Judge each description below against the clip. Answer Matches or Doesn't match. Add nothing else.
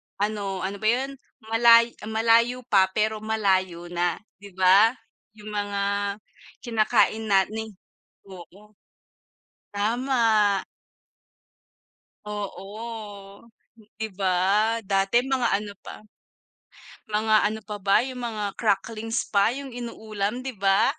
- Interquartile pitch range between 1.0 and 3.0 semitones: Matches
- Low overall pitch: Doesn't match